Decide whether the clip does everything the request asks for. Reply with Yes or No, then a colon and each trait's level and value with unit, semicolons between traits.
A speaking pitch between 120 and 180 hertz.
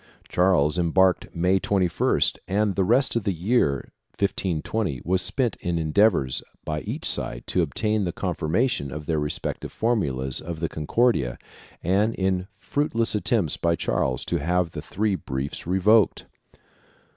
No: very low, 90 Hz